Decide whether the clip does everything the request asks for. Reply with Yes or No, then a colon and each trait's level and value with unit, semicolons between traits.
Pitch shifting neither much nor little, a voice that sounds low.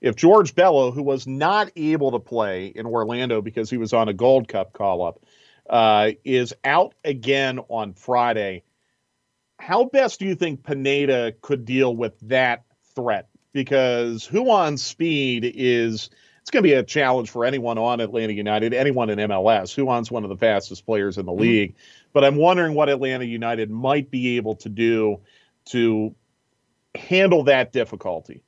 Yes: average, 3.6 semitones; low, 125 Hz